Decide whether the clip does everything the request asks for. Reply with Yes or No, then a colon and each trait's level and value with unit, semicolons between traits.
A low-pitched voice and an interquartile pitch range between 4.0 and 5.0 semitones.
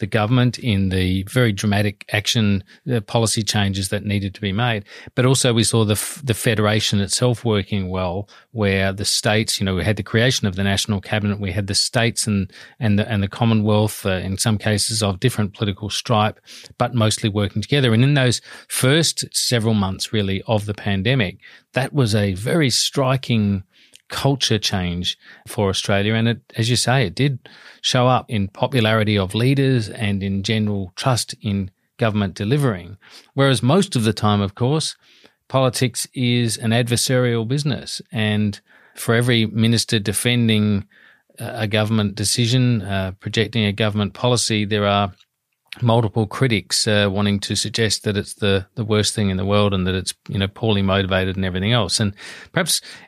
No: low, 110 Hz; average, 3.2 semitones